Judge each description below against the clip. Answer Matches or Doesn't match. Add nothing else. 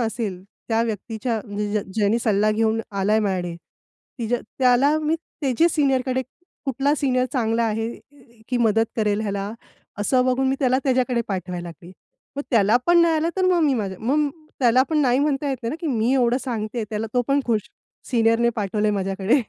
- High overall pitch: Matches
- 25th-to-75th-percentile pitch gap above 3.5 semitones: Matches